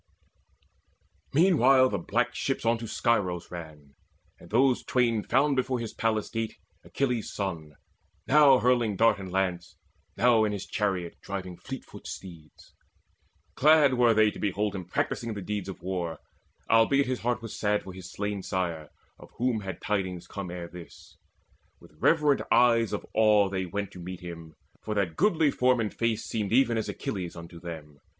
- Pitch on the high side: No, low, 105 Hz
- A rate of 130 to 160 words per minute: No, average, 170 wpm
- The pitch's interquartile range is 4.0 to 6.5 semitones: Yes, average, 5.0 semitones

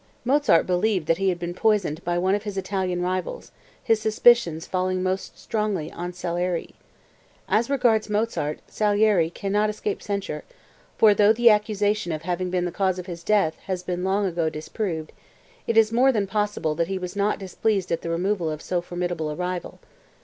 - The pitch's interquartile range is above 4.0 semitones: No, average, 3.3 semitones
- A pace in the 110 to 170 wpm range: No, average, 185 wpm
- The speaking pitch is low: No, medium, 185 Hz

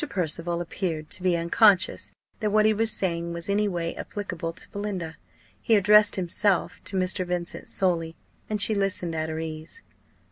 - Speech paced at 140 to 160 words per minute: No, average, 170 wpm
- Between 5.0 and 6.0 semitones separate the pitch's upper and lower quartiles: No, average, 3.4 semitones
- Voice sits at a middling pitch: Yes, medium, 180 Hz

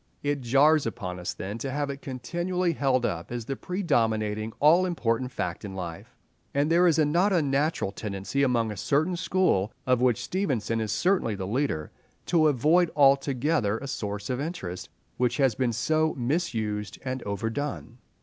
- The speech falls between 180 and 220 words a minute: No, average, 170 wpm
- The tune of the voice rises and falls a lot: Yes, wide, 6.0 semitones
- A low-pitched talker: Yes, low, 130 Hz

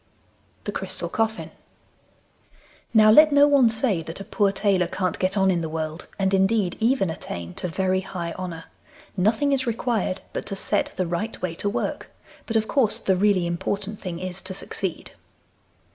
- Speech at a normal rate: Yes, average, 175 wpm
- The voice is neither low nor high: No, high, 195 Hz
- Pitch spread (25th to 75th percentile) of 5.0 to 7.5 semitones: No, average, 3.6 semitones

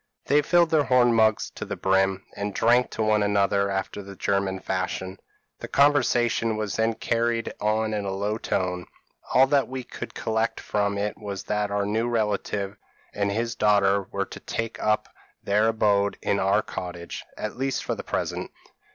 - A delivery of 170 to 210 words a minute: Yes, average, 180 wpm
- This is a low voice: Yes, low, 105 Hz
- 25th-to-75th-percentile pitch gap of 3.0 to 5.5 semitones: No, narrow, 2.5 semitones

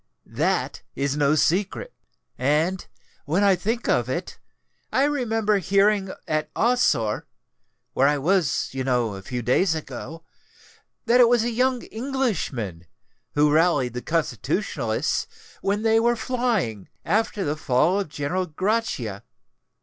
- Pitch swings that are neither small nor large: No, wide, 8.1 semitones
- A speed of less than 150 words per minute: Yes, slow, 135 wpm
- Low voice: No, medium, 180 Hz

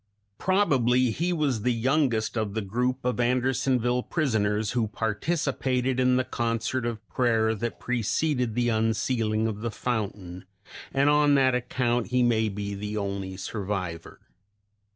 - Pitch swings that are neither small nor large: Yes, average, 3.0 semitones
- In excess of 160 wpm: No, average, 140 wpm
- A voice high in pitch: No, low, 120 Hz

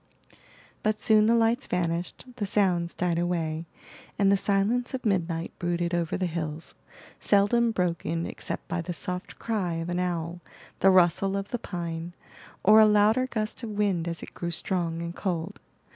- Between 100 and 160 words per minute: No, average, 170 wpm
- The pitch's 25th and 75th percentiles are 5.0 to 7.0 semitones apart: No, average, 3.6 semitones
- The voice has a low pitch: No, medium, 180 Hz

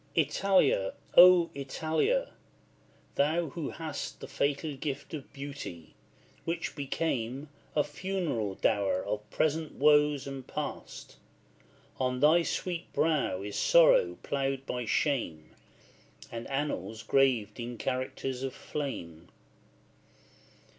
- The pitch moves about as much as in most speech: Yes, average, 4.5 semitones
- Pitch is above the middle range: No, medium, 140 Hz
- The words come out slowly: Yes, slow, 105 wpm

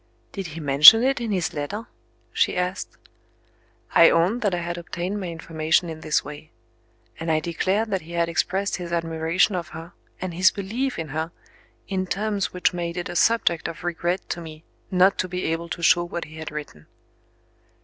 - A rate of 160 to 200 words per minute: Yes, average, 190 wpm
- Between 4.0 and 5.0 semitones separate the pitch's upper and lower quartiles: No, average, 2.7 semitones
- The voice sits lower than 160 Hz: No, medium, 175 Hz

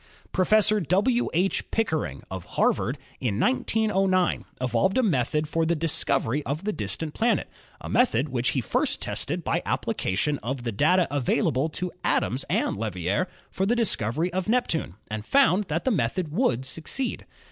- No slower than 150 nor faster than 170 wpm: Yes, average, 160 wpm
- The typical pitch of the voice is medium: Yes, medium, 160 Hz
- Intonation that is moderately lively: No, wide, 7.6 semitones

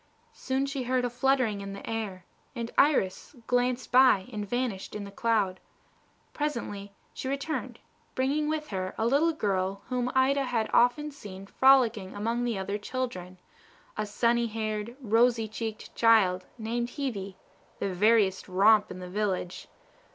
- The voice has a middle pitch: No, high, 225 Hz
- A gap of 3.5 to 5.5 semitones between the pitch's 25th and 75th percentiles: Yes, average, 4.4 semitones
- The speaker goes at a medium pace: Yes, average, 150 wpm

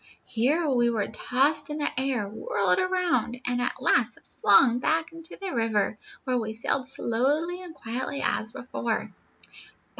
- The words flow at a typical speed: Yes, average, 150 wpm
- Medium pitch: No, very high, 250 Hz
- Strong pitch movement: No, average, 5.0 semitones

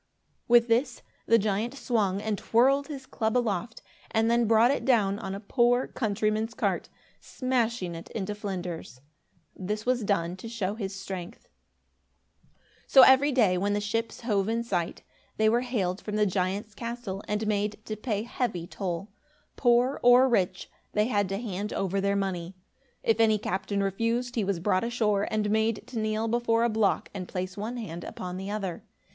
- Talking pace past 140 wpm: Yes, average, 175 wpm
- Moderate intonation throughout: Yes, average, 3.2 semitones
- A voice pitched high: Yes, high, 215 Hz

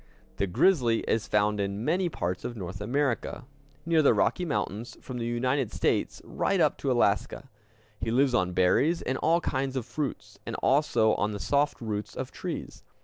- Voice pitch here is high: No, low, 120 Hz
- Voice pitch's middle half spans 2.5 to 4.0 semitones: No, average, 5.3 semitones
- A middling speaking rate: Yes, average, 180 wpm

